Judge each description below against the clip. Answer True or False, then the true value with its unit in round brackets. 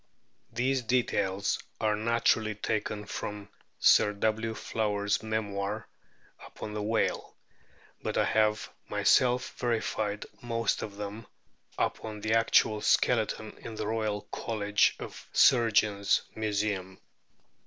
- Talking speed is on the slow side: True (110 wpm)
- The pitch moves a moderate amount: False (1.5 semitones)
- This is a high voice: False (110 Hz)